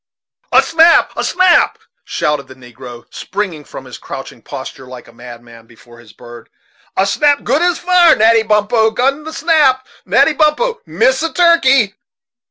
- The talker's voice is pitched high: Yes, high, 220 Hz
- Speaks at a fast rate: No, average, 160 wpm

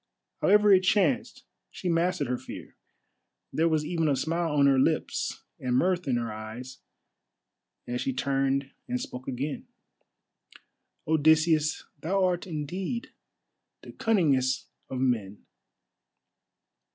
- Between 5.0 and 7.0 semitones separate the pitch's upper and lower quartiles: Yes, average, 5.3 semitones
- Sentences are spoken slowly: Yes, slow, 120 wpm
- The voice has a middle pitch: Yes, medium, 150 Hz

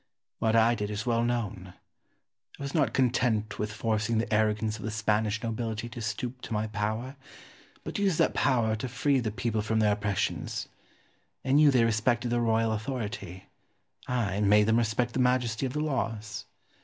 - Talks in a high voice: No, low, 110 Hz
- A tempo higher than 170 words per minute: Yes, average, 180 wpm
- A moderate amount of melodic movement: No, narrow, 2.3 semitones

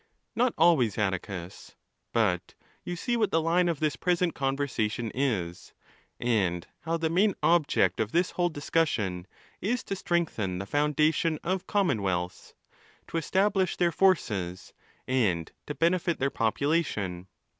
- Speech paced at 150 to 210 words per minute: No, average, 140 wpm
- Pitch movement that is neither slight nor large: No, wide, 9.0 semitones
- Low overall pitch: No, medium, 145 Hz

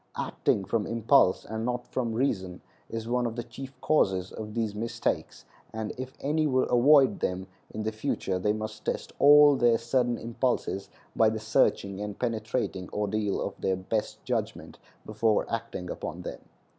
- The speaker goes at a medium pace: Yes, average, 165 wpm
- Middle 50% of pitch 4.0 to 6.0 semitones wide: No, average, 2.9 semitones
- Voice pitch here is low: Yes, low, 110 Hz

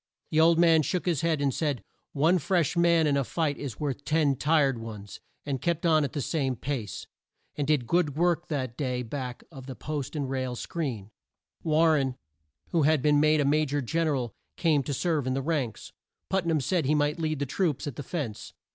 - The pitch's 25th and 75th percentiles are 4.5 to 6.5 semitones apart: No, average, 3.3 semitones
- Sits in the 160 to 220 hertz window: No, medium, 145 Hz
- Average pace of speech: No, fast, 220 wpm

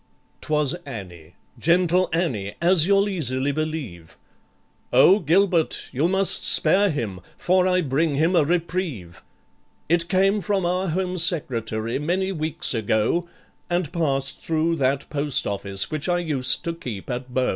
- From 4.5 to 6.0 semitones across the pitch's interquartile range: Yes, wide, 5.6 semitones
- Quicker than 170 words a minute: No, average, 145 wpm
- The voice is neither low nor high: Yes, medium, 155 Hz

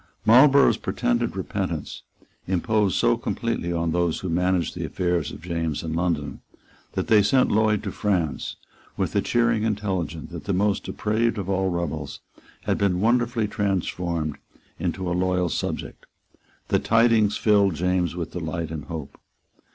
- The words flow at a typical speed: Yes, average, 150 wpm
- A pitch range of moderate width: Yes, average, 3.9 semitones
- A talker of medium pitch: No, very low, 90 Hz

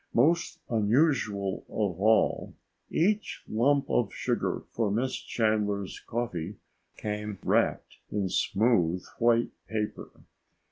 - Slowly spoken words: Yes, slow, 100 wpm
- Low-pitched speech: Yes, low, 110 Hz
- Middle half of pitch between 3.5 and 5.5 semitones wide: No, average, 3.1 semitones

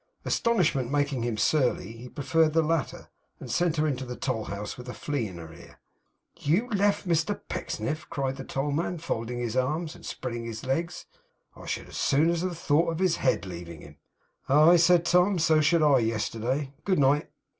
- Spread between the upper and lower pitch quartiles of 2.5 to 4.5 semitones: No, average, 5.3 semitones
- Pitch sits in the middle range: Yes, medium, 145 Hz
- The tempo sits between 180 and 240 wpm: Yes, average, 190 wpm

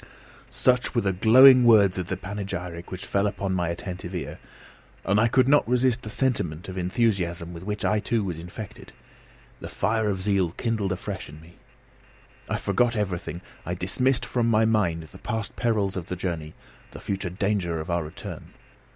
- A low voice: Yes, low, 100 Hz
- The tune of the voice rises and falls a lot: No, average, 4.1 semitones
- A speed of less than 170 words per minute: No, average, 175 wpm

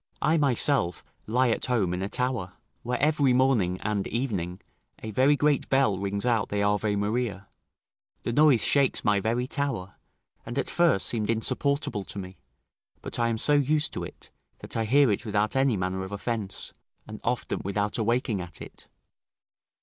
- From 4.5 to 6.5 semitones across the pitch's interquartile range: Yes, average, 4.8 semitones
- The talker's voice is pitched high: No, low, 115 Hz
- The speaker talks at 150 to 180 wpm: Yes, average, 175 wpm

